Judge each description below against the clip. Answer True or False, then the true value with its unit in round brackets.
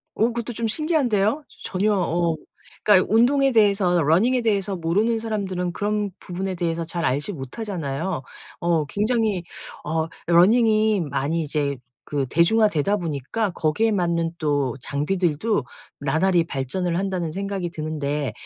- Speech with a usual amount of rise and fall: True (5.0 semitones)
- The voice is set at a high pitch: False (180 Hz)